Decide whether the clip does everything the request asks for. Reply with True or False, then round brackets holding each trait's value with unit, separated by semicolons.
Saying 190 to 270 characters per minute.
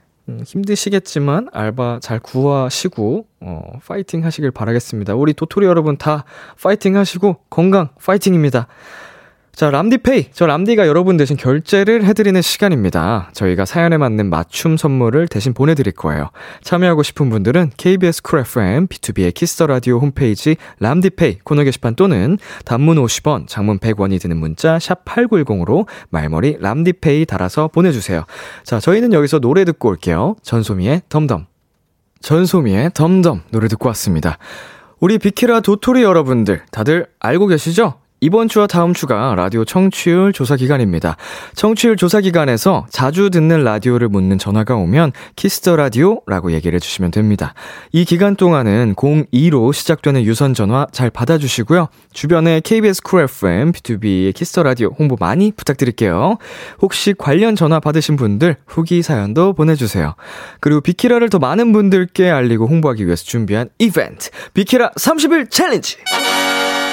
False (350 characters per minute)